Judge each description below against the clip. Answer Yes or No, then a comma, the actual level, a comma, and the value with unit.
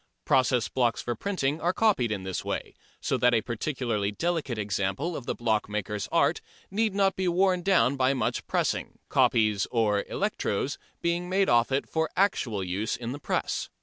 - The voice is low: Yes, low, 125 Hz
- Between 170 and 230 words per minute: Yes, average, 175 wpm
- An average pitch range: No, wide, 8.2 semitones